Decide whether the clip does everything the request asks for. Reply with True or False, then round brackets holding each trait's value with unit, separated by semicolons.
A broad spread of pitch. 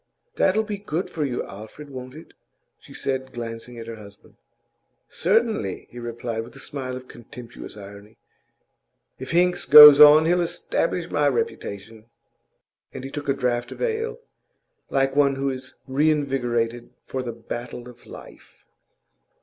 False (4.2 semitones)